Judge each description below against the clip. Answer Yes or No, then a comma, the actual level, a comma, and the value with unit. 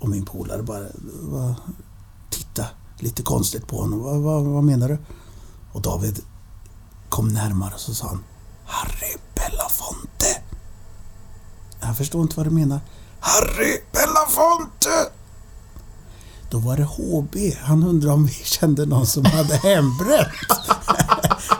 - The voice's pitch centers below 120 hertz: Yes, low, 110 Hz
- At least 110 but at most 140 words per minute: Yes, average, 130 wpm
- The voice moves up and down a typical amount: No, wide, 7.1 semitones